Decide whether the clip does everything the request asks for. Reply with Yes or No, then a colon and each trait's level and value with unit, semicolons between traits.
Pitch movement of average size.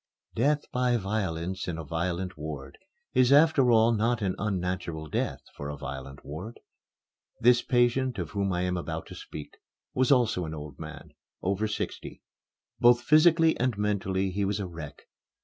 No: wide, 6.6 semitones